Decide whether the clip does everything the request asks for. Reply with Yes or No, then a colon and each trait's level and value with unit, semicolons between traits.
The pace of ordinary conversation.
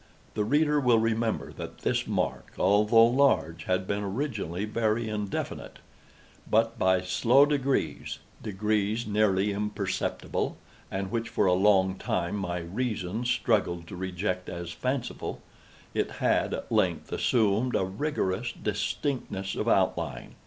No: slow, 125 wpm